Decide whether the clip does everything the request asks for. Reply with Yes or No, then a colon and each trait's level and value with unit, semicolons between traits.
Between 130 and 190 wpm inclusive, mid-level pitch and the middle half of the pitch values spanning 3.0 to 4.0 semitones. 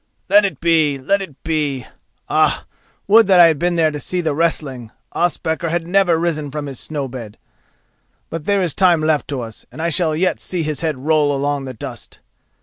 No: average, 200 wpm; medium, 155 Hz; average, 3.3 semitones